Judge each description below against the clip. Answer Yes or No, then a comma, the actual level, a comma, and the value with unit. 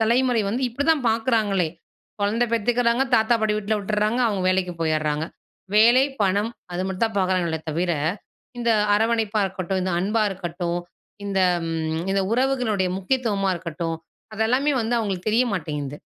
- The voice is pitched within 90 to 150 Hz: No, high, 205 Hz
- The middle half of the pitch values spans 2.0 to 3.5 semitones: No, average, 4.2 semitones